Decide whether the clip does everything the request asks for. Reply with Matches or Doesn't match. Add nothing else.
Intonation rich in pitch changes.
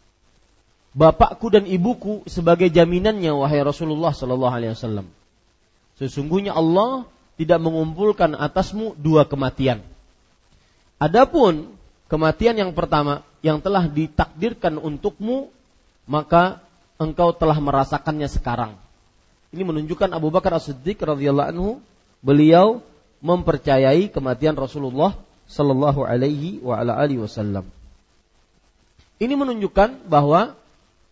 Matches